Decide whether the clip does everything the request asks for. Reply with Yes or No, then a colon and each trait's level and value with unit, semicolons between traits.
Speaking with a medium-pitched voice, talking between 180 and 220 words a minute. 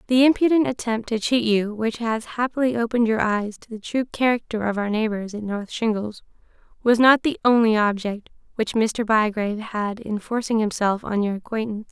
No: high, 225 Hz; average, 185 wpm